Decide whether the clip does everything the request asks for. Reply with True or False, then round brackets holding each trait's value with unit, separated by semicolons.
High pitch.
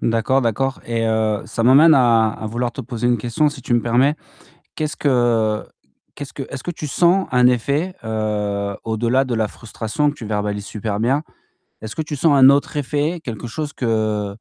False (120 Hz)